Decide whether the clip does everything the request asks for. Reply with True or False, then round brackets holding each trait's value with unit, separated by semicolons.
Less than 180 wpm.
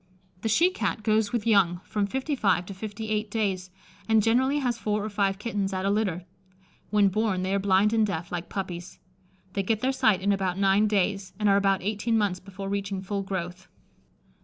False (205 wpm)